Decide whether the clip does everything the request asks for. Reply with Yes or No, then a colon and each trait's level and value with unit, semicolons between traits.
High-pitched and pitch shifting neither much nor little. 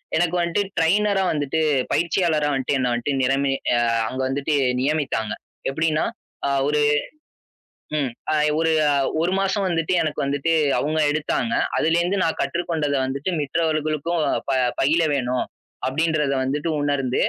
No: medium, 155 Hz; average, 3.2 semitones